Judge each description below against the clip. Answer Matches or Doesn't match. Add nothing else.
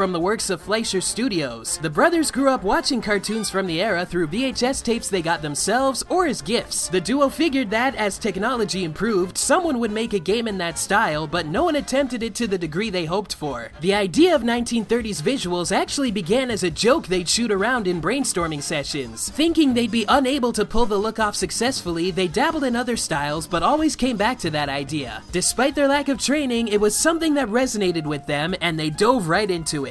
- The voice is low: Doesn't match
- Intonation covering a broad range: Matches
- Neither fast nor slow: Doesn't match